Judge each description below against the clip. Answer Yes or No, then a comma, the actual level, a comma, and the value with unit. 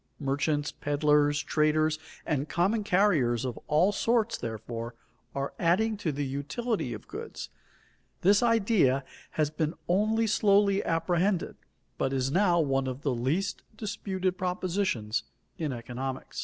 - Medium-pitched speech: Yes, medium, 155 Hz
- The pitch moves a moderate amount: No, wide, 6.5 semitones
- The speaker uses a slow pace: Yes, slow, 130 wpm